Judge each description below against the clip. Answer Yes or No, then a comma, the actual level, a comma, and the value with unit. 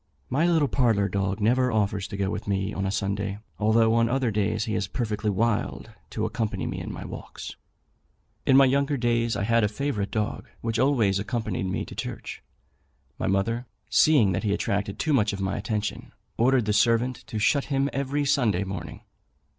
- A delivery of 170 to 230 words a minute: Yes, average, 190 wpm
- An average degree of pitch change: Yes, average, 4.0 semitones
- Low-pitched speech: Yes, low, 110 Hz